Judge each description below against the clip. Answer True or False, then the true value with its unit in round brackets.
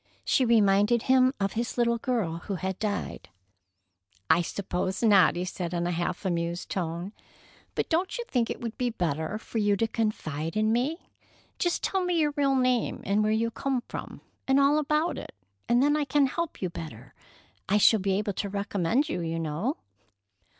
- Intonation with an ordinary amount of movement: False (6.1 semitones)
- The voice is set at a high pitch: True (215 Hz)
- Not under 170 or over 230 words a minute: True (190 wpm)